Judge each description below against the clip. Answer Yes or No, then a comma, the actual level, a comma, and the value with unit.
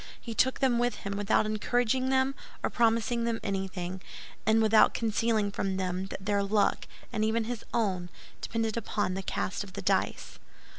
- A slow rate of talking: No, average, 175 wpm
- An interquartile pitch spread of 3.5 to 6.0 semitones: No, average, 2.8 semitones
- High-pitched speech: Yes, high, 215 Hz